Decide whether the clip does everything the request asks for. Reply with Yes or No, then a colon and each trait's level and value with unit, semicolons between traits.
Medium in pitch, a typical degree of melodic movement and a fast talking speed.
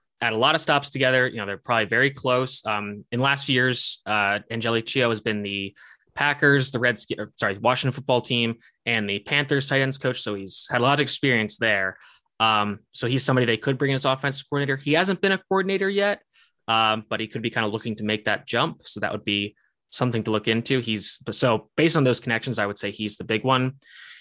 No: low, 125 Hz; average, 3.8 semitones; fast, 230 wpm